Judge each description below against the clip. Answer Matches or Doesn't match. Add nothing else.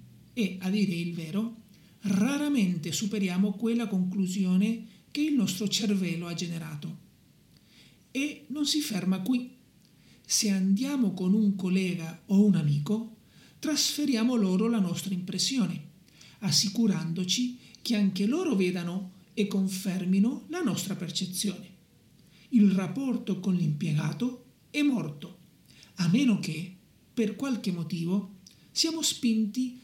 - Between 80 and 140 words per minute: Matches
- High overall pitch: Matches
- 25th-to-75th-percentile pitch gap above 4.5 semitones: Doesn't match